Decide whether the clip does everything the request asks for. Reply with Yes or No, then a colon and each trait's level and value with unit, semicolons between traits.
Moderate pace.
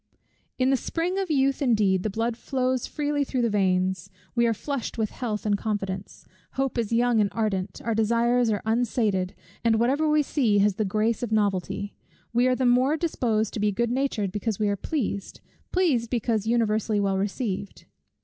Yes: average, 185 wpm